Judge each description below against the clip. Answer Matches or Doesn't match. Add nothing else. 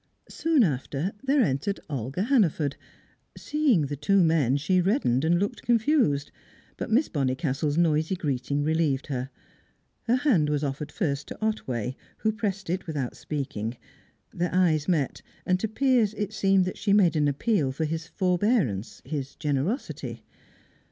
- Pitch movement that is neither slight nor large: Doesn't match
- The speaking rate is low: Doesn't match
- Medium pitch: Matches